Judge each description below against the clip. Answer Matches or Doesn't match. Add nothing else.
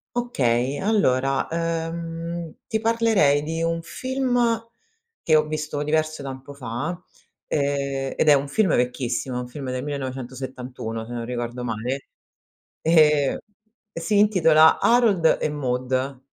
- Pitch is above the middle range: Doesn't match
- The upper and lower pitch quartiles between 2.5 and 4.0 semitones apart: Doesn't match